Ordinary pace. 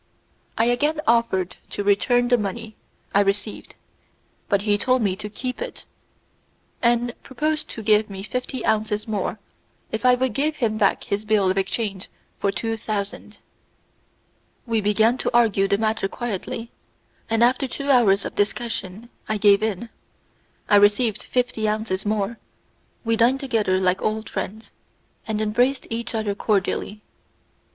Yes: average, 150 wpm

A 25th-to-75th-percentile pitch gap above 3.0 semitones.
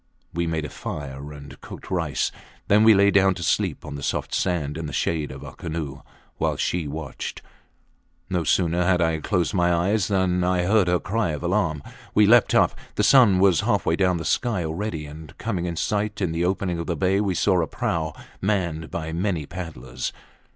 Yes: average, 3.4 semitones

